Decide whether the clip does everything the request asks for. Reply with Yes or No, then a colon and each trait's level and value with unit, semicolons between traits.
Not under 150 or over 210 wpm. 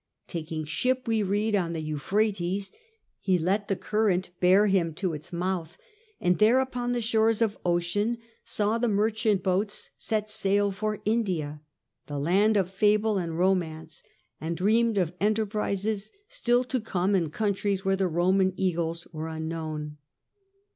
Yes: average, 155 wpm